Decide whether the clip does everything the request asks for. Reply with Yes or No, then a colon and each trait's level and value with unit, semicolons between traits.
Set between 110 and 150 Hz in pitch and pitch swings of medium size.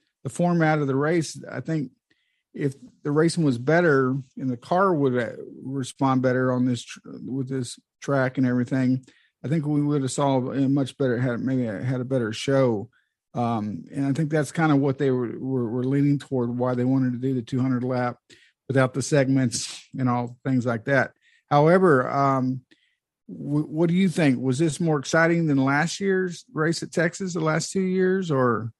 Yes: low, 135 Hz; average, 3.2 semitones